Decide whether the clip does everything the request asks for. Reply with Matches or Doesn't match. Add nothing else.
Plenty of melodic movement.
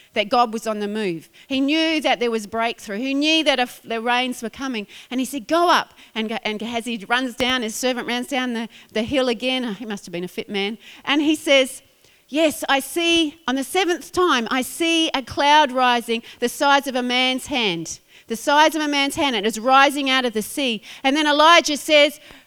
Doesn't match